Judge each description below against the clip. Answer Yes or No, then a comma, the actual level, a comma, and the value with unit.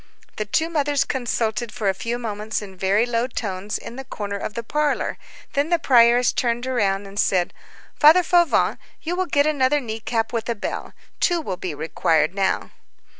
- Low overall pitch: No, high, 235 Hz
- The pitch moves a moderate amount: No, wide, 5.8 semitones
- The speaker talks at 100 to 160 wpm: No, average, 185 wpm